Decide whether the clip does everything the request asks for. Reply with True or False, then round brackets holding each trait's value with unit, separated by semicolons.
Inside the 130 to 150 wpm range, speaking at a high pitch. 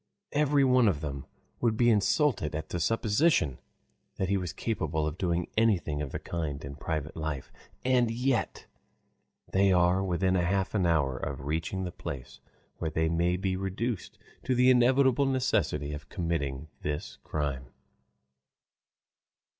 False (145 wpm; 90 Hz)